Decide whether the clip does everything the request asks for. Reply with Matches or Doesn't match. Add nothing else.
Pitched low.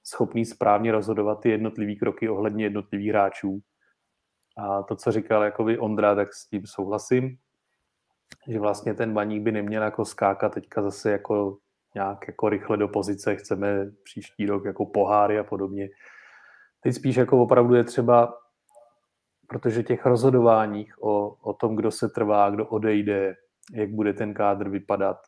Matches